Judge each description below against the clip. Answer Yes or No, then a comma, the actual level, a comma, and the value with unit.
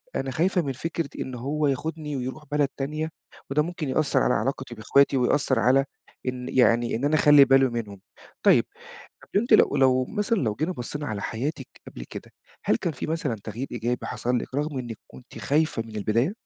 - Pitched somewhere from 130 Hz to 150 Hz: Yes, low, 135 Hz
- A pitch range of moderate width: Yes, average, 3.9 semitones